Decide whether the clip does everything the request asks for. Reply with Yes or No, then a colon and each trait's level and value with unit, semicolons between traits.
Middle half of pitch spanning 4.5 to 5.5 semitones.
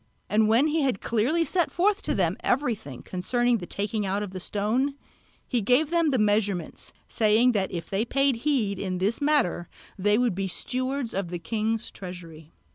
Yes: average, 5.2 semitones